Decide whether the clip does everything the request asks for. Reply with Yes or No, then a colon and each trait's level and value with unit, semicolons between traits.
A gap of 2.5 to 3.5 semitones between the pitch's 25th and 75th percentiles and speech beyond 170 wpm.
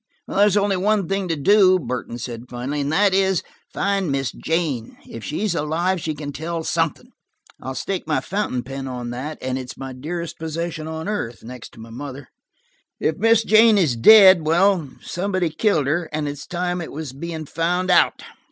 No: wide, 5.5 semitones; average, 180 wpm